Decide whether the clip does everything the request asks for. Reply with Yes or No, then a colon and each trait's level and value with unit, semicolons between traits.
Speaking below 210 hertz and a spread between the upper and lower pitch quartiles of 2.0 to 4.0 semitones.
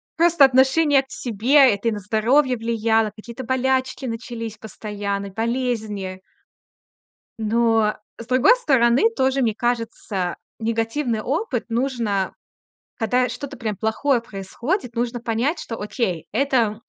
No: high, 235 Hz; average, 3.2 semitones